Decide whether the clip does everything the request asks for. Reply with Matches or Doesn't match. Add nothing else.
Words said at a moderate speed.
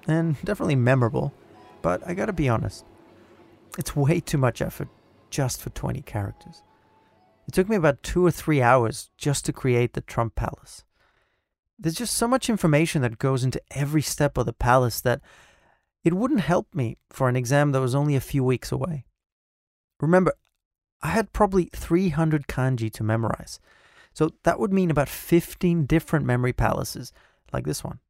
Matches